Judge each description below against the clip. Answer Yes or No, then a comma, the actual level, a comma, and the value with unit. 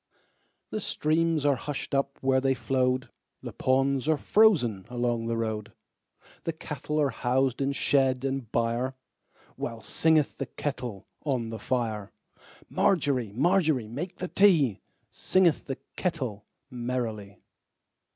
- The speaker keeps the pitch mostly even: No, average, 3.9 semitones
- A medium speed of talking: No, slow, 110 wpm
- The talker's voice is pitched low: Yes, low, 130 Hz